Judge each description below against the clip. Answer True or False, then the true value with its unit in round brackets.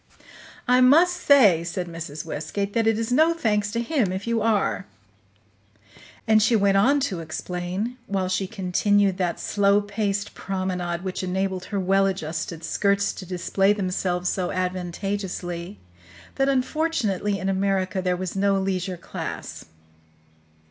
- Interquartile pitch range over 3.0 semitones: False (2.5 semitones)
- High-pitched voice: True (195 Hz)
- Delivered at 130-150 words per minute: True (140 wpm)